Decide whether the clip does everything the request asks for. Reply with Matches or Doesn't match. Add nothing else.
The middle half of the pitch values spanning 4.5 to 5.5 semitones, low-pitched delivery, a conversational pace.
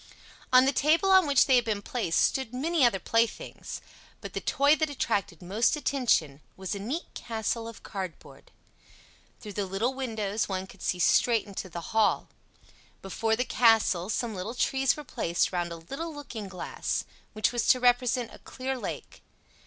Doesn't match